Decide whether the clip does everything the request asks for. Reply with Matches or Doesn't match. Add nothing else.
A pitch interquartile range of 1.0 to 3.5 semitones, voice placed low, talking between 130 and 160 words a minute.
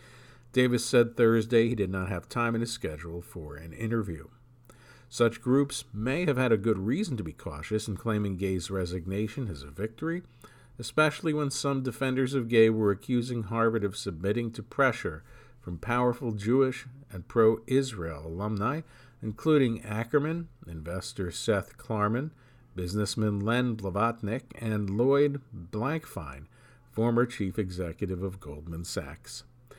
Doesn't match